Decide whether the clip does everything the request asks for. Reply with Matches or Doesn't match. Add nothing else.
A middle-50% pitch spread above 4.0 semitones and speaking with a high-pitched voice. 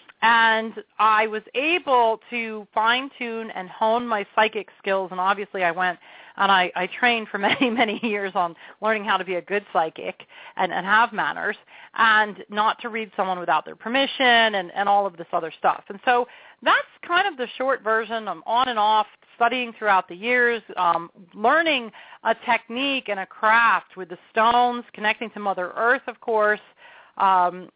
Doesn't match